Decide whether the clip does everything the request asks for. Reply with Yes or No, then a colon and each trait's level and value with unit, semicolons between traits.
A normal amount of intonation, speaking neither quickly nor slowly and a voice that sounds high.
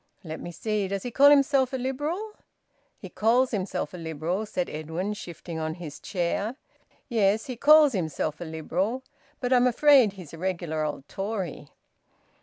No: wide, 7.1 semitones; average, 165 wpm; high, 195 Hz